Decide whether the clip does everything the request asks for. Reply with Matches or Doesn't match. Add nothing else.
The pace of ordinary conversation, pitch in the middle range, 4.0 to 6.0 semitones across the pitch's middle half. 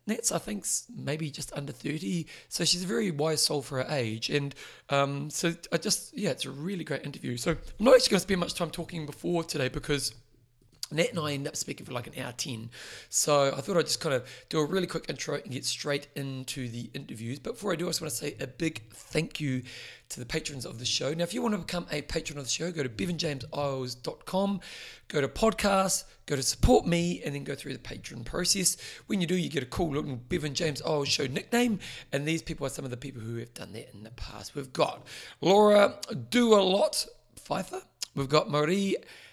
Doesn't match